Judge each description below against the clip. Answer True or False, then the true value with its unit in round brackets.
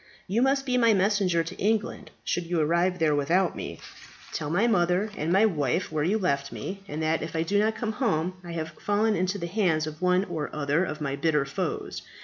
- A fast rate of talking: True (215 wpm)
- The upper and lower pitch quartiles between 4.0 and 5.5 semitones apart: True (4.6 semitones)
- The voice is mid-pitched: True (175 Hz)